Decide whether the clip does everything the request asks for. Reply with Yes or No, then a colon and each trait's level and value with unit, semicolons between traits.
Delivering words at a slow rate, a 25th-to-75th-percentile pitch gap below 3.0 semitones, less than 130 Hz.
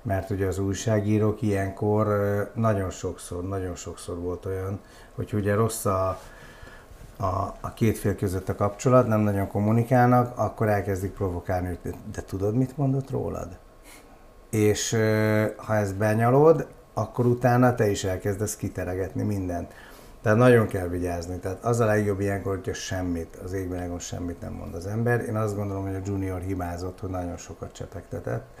No: fast, 155 wpm; narrow, 2.6 semitones; low, 100 Hz